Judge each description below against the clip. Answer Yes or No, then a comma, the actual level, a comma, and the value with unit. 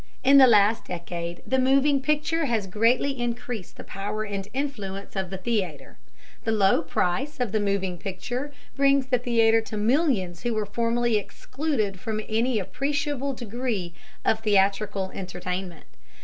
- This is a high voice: Yes, high, 220 Hz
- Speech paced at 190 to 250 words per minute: No, average, 150 wpm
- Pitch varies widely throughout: No, average, 4.9 semitones